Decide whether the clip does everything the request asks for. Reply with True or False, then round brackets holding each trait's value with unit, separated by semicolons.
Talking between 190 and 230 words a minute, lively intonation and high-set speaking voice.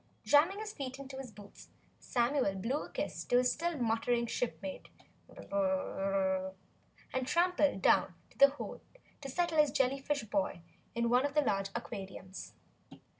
False (145 wpm; 6.5 semitones; 250 Hz)